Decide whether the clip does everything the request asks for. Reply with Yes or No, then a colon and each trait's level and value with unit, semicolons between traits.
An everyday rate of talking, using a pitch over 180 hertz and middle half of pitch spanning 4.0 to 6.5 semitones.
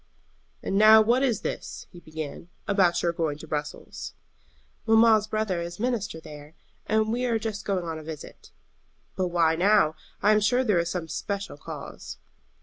Yes: average, 170 wpm; high, 190 Hz; average, 5.1 semitones